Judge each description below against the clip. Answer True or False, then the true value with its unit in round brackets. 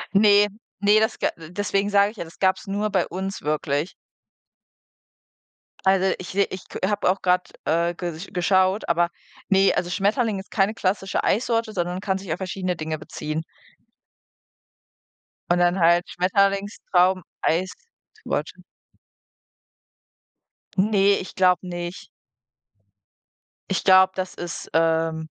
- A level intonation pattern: True (2.2 semitones)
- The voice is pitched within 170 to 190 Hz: True (185 Hz)